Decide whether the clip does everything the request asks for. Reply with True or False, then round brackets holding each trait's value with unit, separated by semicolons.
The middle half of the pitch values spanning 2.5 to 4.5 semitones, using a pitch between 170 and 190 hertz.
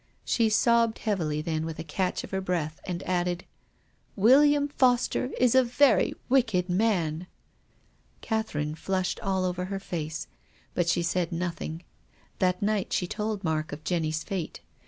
False (4.9 semitones; 185 Hz)